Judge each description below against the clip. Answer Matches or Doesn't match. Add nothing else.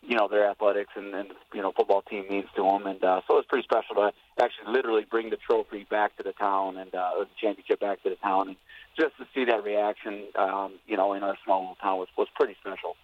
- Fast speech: Matches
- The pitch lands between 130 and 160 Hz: Doesn't match